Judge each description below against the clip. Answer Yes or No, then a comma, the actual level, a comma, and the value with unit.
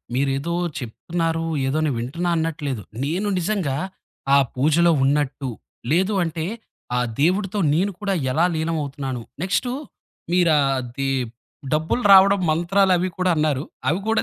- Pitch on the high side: No, medium, 165 Hz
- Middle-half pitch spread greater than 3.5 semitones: Yes, average, 4.8 semitones